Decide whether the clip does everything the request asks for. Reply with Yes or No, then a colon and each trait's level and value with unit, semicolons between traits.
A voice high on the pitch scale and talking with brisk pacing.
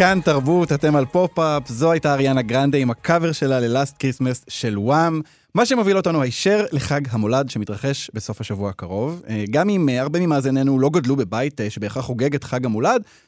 No: low, 135 Hz; fast, 170 wpm